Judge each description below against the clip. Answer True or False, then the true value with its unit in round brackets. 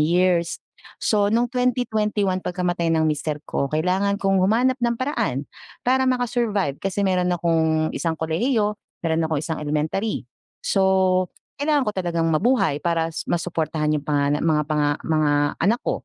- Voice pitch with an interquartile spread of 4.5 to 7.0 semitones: True (5.0 semitones)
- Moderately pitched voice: True (180 Hz)